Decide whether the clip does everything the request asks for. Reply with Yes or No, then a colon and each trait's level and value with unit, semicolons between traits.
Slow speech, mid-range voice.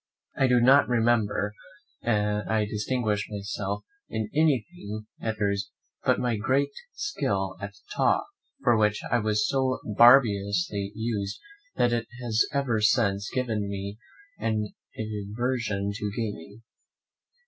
No: slow, 130 wpm; low, 110 Hz